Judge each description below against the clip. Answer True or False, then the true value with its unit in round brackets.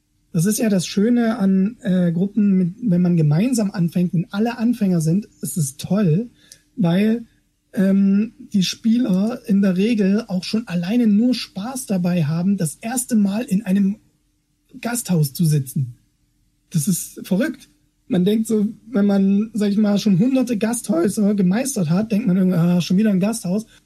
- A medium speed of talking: True (165 wpm)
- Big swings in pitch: False (3.5 semitones)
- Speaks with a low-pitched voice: False (200 Hz)